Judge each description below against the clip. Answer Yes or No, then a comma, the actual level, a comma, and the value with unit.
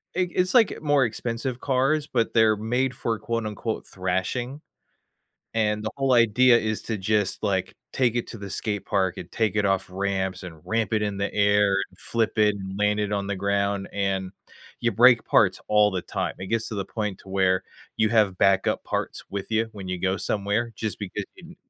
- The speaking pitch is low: Yes, low, 105 Hz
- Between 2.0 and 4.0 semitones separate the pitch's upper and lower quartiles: Yes, average, 2.9 semitones